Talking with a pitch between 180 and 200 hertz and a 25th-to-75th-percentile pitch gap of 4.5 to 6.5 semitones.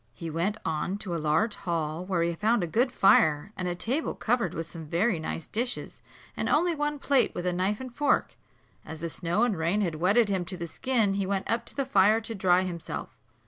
Yes: high, 190 Hz; average, 5.2 semitones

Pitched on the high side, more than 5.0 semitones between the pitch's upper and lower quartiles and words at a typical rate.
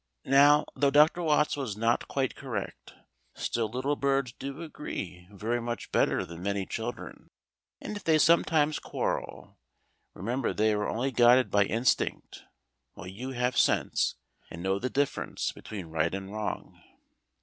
No: low, 120 Hz; wide, 5.4 semitones; average, 150 wpm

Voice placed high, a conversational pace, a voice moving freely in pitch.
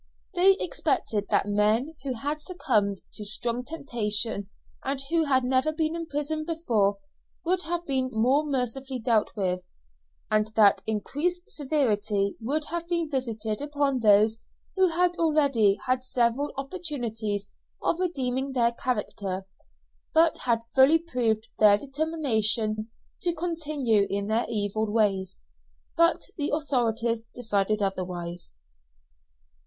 No: very high, 250 Hz; slow, 125 wpm; wide, 6.0 semitones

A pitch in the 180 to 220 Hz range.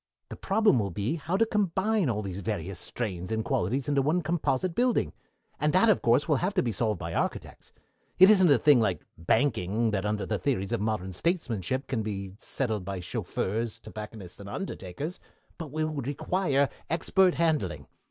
No: low, 125 Hz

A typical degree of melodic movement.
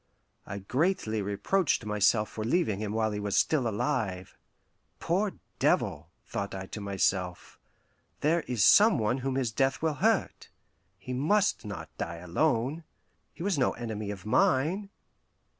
No: wide, 6.9 semitones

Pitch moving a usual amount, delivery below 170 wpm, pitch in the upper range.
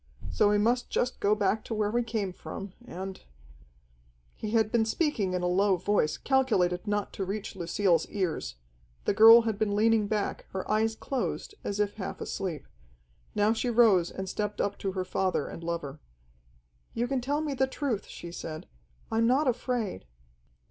No: average, 3.7 semitones; average, 180 wpm; high, 205 Hz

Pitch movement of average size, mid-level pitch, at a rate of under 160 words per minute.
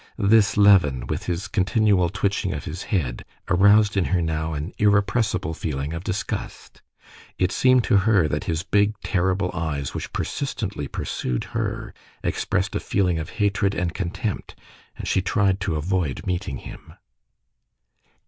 No: average, 3.8 semitones; very low, 95 Hz; average, 150 wpm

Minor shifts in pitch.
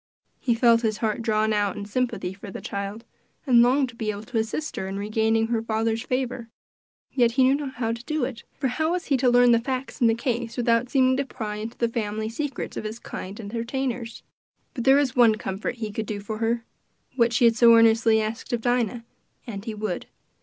Yes: narrow, 2.3 semitones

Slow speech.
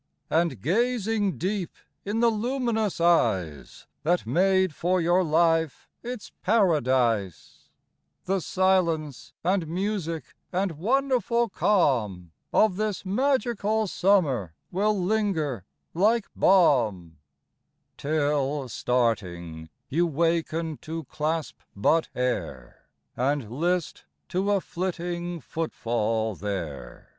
Yes: slow, 105 wpm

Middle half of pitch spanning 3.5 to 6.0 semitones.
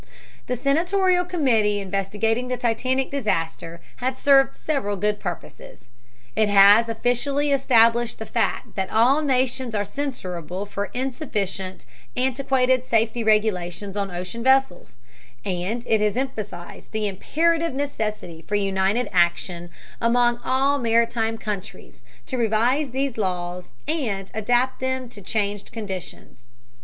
Yes: average, 4.7 semitones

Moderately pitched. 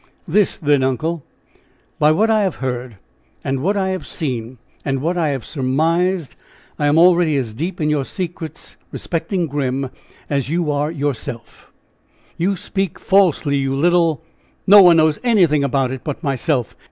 Yes: medium, 155 Hz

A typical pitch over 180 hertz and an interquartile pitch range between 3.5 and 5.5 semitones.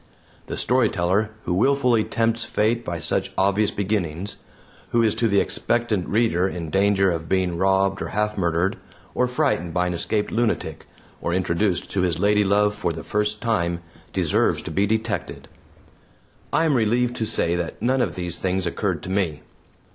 No: low, 100 Hz; average, 3.9 semitones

